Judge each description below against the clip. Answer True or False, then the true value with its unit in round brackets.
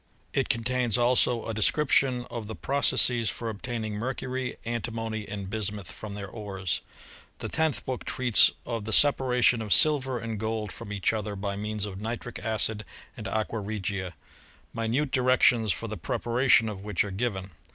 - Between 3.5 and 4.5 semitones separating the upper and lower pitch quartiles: False (3.0 semitones)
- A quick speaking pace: False (165 wpm)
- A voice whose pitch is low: True (110 Hz)